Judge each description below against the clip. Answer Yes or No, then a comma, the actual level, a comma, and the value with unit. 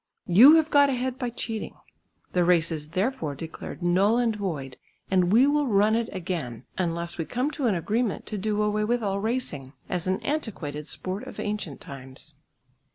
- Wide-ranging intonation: Yes, wide, 5.9 semitones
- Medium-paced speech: Yes, average, 180 wpm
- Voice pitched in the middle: No, high, 200 Hz